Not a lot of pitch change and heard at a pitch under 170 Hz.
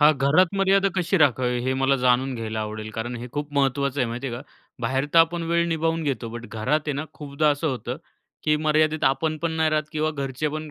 No: average, 3.8 semitones; medium, 140 Hz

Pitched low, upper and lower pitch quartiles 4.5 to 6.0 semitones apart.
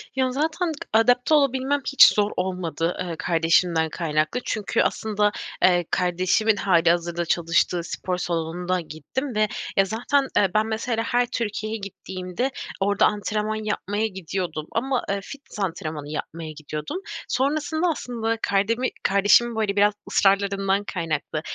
No: high, 200 Hz; average, 4.8 semitones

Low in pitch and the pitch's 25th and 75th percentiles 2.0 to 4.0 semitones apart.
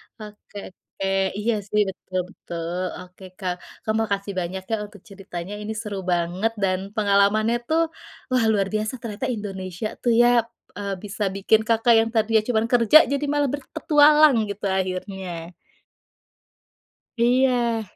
No: high, 210 Hz; average, 3.2 semitones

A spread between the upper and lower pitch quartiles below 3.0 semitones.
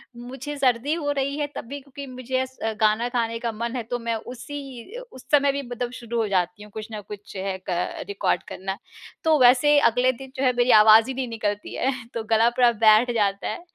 No: average, 3.4 semitones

